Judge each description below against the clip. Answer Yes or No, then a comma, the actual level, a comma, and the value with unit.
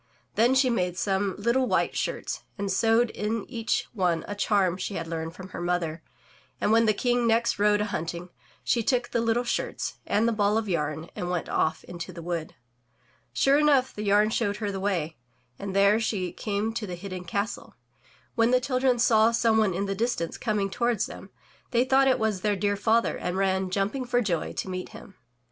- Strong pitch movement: No, average, 4.0 semitones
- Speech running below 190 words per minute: No, fast, 205 wpm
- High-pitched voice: Yes, high, 205 Hz